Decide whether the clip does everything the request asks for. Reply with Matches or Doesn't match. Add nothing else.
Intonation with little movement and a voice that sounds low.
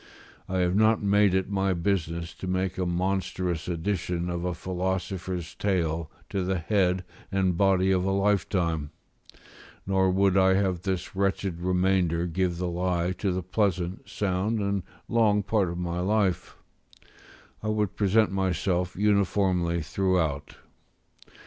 Matches